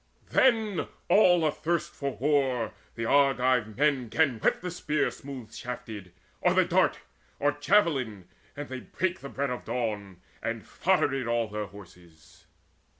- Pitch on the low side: Yes, low, 130 Hz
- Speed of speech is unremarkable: Yes, average, 145 wpm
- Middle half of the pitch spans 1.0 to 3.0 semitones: No, average, 5.2 semitones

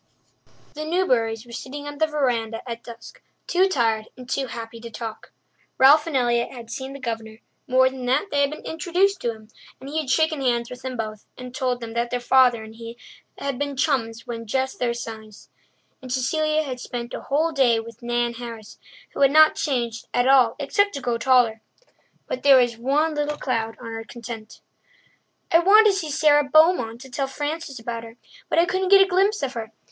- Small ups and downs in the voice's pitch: No, average, 4.1 semitones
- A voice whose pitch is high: Yes, very high, 255 Hz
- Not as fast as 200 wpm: No, fast, 205 wpm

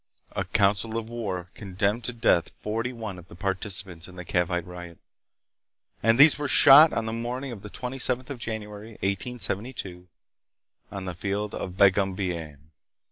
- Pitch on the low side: Yes, low, 100 Hz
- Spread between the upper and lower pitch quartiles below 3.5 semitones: No, average, 4.2 semitones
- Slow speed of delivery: No, average, 155 wpm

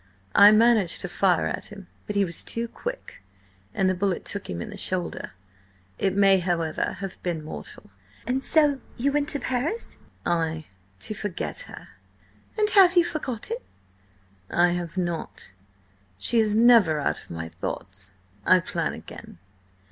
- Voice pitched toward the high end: Yes, high, 195 Hz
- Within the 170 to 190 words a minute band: No, average, 155 wpm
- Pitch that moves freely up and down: Yes, wide, 6.2 semitones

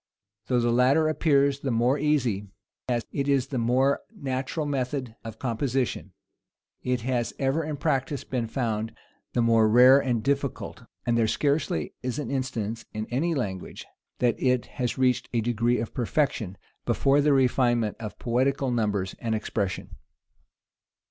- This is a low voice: Yes, low, 125 Hz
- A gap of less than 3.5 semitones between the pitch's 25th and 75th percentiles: Yes, average, 3.1 semitones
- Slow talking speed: No, average, 150 wpm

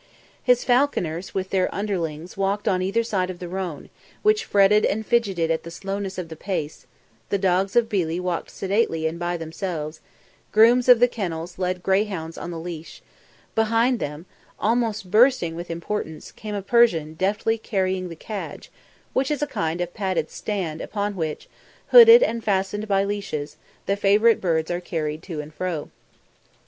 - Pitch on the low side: No, high, 190 Hz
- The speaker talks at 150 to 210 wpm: Yes, average, 170 wpm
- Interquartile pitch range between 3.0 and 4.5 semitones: Yes, average, 4.2 semitones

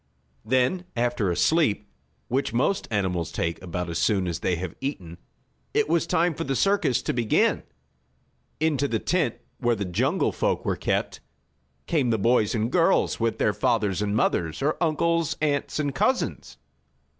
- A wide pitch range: Yes, wide, 7.1 semitones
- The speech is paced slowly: No, average, 165 wpm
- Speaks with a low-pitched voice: Yes, low, 115 Hz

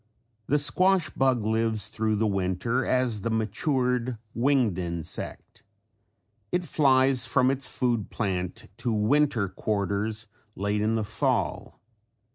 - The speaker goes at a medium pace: No, slow, 125 wpm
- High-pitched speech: No, low, 115 Hz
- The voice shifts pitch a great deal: No, average, 3.7 semitones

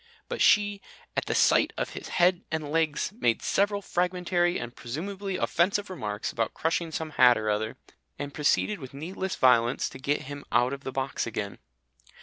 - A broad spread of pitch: Yes, wide, 6.3 semitones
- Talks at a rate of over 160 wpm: Yes, average, 175 wpm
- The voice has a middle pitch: Yes, medium, 155 Hz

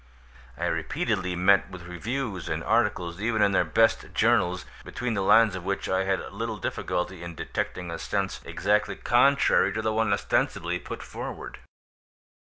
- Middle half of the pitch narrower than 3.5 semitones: No, average, 3.8 semitones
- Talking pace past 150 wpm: Yes, average, 160 wpm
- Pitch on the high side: No, low, 100 Hz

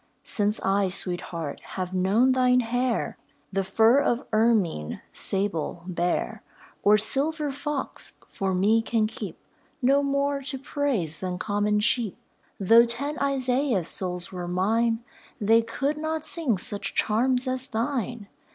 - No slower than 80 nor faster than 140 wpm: Yes, slow, 135 wpm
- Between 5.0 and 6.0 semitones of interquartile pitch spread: Yes, average, 5.3 semitones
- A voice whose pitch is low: No, high, 225 Hz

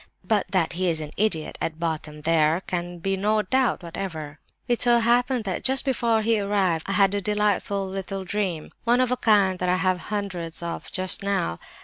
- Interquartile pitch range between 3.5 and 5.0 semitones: Yes, average, 3.8 semitones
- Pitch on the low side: No, high, 195 Hz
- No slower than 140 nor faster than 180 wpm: No, average, 200 wpm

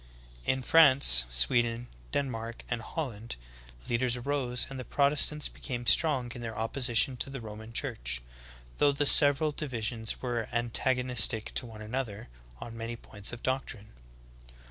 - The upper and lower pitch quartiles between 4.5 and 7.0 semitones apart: No, average, 3.0 semitones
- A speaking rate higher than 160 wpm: No, average, 145 wpm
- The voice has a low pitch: Yes, low, 120 Hz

